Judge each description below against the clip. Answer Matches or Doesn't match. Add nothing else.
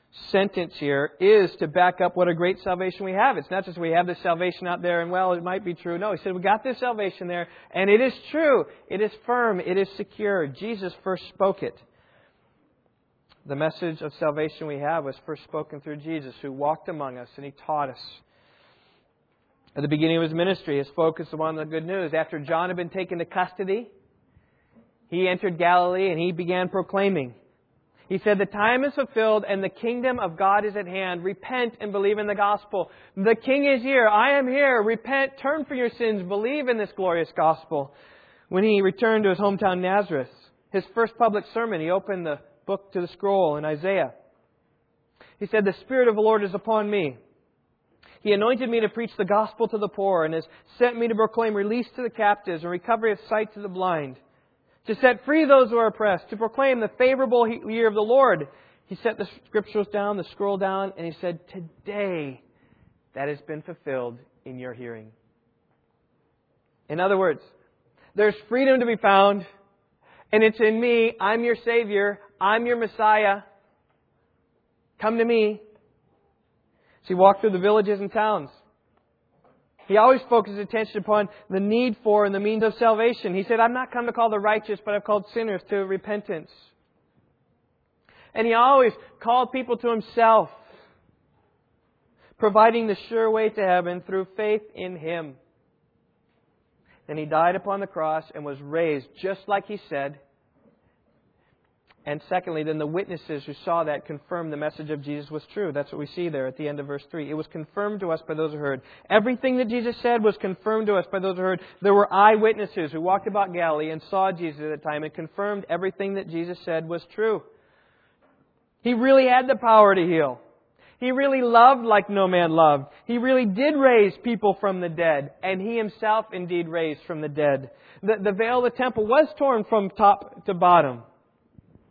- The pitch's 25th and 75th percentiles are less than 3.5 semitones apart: Doesn't match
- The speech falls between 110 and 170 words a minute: Doesn't match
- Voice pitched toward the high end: Matches